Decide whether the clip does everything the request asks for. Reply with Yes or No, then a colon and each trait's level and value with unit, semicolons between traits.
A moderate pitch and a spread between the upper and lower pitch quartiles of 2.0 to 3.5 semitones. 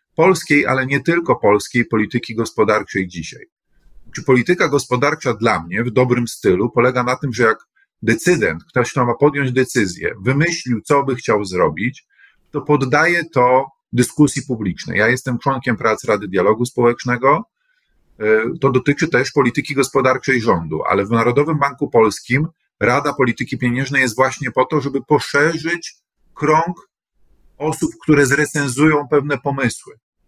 No: low, 130 Hz; average, 3.2 semitones